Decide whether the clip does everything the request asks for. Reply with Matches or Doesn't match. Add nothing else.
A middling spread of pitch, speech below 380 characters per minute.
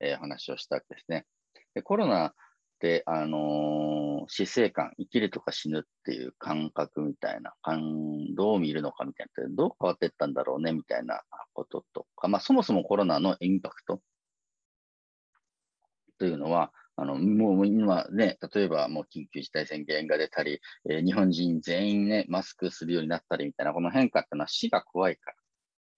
Matches